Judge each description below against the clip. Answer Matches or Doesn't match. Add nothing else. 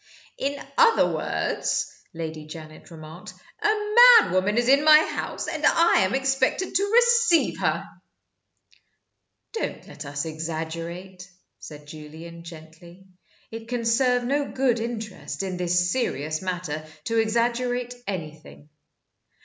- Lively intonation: Matches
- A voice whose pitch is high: Matches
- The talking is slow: Matches